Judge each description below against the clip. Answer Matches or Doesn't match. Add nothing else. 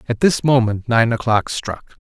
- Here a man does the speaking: Matches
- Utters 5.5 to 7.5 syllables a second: Doesn't match